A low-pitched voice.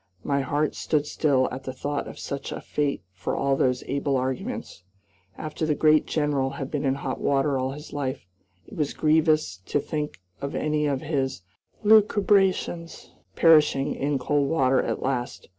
No: medium, 145 Hz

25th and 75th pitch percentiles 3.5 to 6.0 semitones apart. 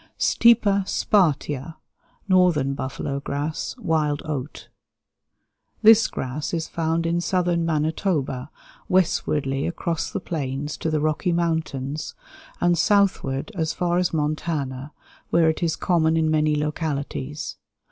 No: average, 3.0 semitones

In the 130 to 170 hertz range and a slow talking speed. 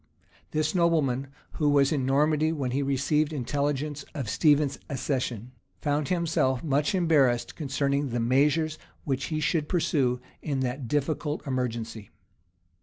Yes: medium, 140 Hz; slow, 130 wpm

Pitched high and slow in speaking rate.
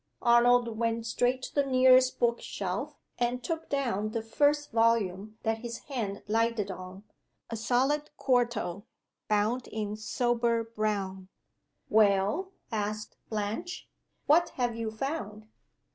Yes: high, 230 Hz; slow, 125 wpm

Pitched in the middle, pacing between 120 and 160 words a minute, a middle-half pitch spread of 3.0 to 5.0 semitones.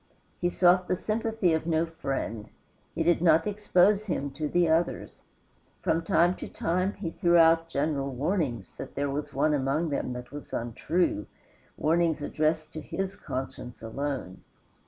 Yes: medium, 160 Hz; average, 155 wpm; average, 3.9 semitones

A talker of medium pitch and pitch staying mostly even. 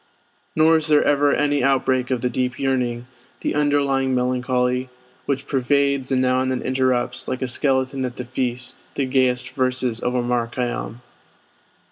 No: low, 130 Hz; narrow, 1.6 semitones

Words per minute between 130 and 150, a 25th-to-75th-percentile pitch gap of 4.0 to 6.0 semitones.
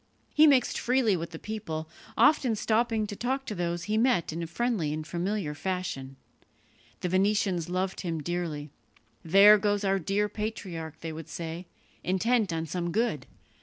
No: average, 160 wpm; average, 4.6 semitones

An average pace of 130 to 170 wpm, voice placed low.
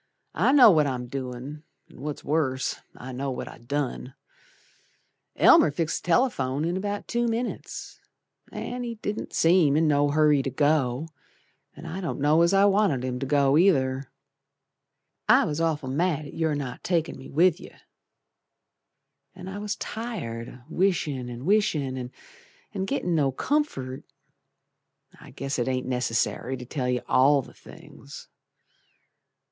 No: average, 150 wpm; medium, 145 Hz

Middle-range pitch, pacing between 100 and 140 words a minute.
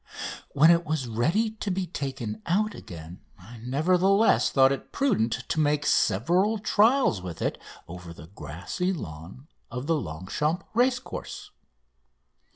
Yes: medium, 145 Hz; slow, 135 wpm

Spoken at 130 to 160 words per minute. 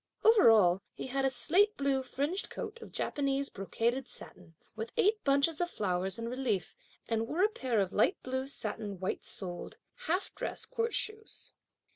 No: average, 170 wpm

